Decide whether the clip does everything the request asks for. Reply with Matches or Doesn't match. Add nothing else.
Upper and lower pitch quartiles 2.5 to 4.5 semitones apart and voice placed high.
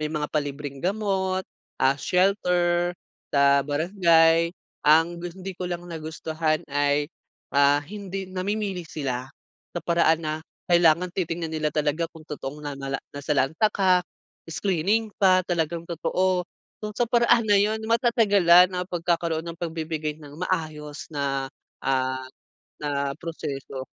Doesn't match